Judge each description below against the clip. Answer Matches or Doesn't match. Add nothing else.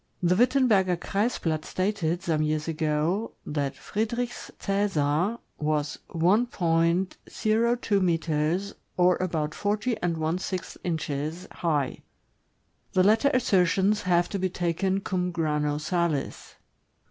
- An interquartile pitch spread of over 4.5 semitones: Doesn't match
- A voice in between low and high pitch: Matches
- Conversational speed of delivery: Doesn't match